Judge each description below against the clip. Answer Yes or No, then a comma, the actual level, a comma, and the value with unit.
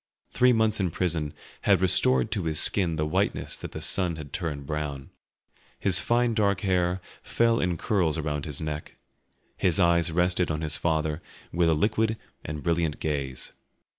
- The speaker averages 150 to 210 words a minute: Yes, average, 165 wpm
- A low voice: Yes, very low, 85 Hz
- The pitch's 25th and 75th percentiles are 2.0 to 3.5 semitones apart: No, average, 3.9 semitones